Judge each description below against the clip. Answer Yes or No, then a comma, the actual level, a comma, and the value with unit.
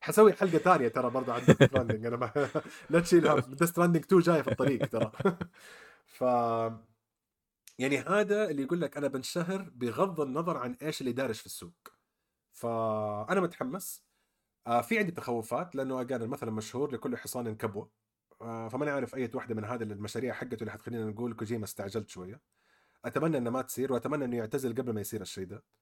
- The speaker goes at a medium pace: No, fast, 165 wpm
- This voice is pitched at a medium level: No, low, 125 Hz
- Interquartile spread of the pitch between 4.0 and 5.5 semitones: Yes, average, 4.6 semitones